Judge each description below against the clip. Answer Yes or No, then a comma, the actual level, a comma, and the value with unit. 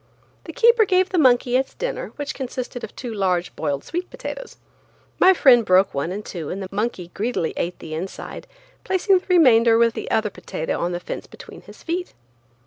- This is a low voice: No, high, 240 Hz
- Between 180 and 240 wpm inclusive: Yes, average, 195 wpm